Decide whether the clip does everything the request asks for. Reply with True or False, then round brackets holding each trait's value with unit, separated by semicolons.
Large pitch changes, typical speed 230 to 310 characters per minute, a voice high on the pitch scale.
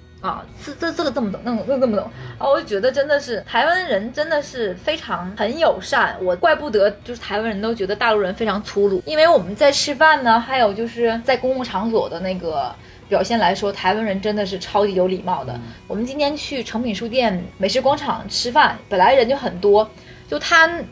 False (6.1 semitones; 325 characters per minute; 225 Hz)